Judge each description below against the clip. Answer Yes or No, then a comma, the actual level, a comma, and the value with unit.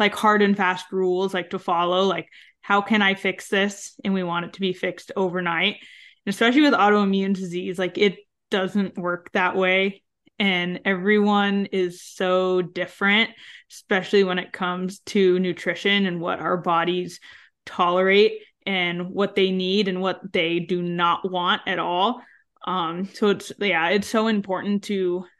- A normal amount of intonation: No, narrow, 2.0 semitones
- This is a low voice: No, high, 190 Hz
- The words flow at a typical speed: Yes, average, 165 wpm